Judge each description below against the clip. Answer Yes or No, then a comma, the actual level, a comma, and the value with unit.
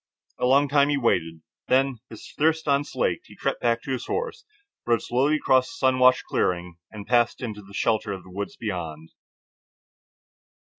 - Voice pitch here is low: Yes, low, 120 Hz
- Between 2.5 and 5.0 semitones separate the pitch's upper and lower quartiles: No, wide, 5.6 semitones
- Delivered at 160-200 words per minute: Yes, average, 170 wpm